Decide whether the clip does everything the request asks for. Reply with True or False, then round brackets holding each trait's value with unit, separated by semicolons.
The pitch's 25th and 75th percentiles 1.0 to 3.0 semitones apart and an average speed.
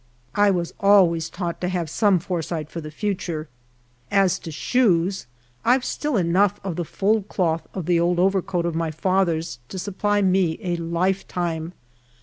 True (2.7 semitones; 165 wpm)